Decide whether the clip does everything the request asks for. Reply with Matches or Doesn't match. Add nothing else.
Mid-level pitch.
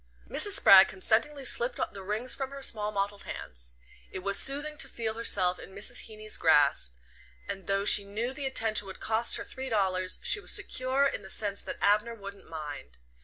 Doesn't match